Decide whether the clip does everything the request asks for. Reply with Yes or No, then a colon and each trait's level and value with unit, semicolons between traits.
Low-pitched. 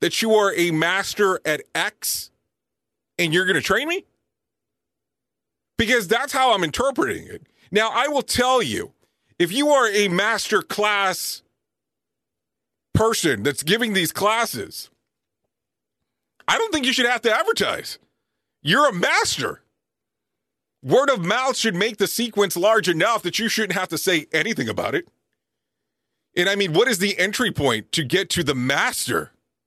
No: high, 215 Hz